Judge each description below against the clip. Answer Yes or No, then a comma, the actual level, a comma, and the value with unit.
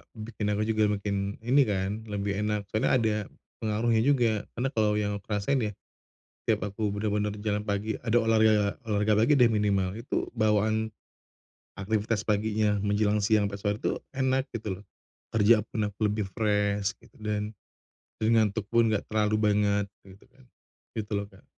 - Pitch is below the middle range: Yes, low, 105 Hz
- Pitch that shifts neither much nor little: No, narrow, 1.3 semitones